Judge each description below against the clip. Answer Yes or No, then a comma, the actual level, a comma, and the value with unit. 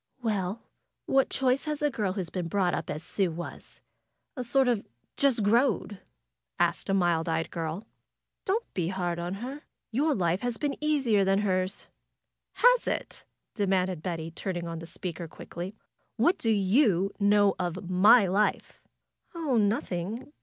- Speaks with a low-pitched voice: No, high, 195 Hz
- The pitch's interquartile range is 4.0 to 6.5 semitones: Yes, wide, 5.6 semitones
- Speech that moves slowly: No, average, 160 wpm